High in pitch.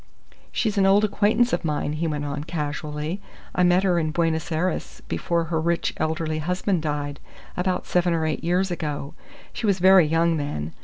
No: medium, 165 Hz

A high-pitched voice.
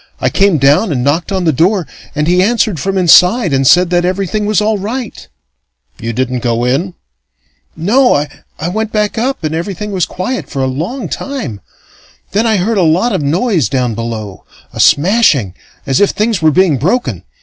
No: medium, 180 Hz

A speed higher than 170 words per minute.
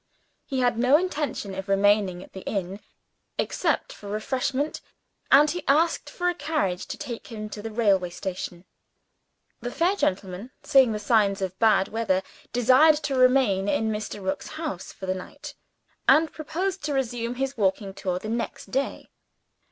No: average, 165 wpm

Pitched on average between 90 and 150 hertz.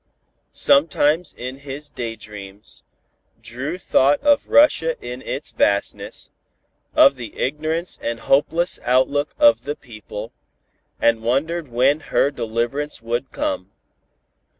Yes: low, 135 Hz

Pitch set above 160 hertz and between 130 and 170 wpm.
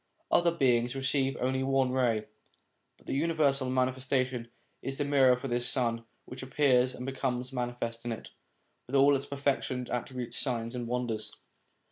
No: low, 130 Hz; average, 155 wpm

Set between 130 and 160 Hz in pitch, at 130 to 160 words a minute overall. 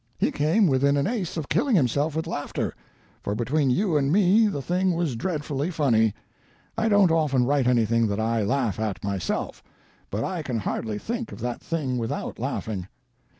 No: medium, 140 Hz; average, 180 wpm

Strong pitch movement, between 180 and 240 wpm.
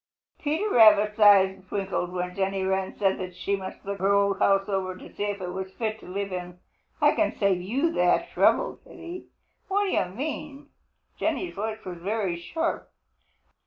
No: average, 2.7 semitones; average, 185 wpm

